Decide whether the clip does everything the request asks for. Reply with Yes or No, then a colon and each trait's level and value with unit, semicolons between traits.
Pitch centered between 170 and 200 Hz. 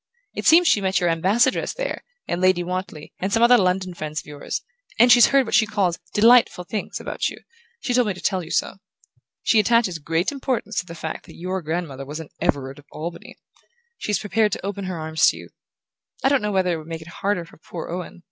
Yes: medium, 185 Hz